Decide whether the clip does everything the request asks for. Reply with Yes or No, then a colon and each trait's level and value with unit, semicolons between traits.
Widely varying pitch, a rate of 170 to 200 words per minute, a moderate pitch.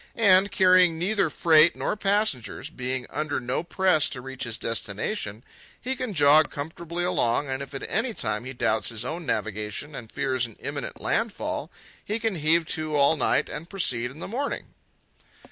Yes: wide, 6.6 semitones; average, 175 wpm; medium, 155 Hz